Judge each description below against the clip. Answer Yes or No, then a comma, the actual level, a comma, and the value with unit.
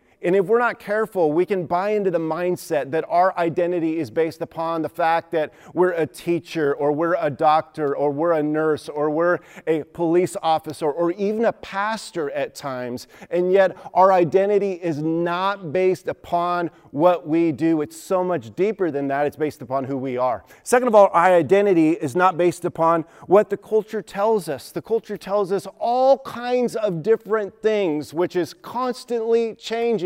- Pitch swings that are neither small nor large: Yes, average, 3.9 semitones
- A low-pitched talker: No, medium, 175 Hz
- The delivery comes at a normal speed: Yes, average, 185 wpm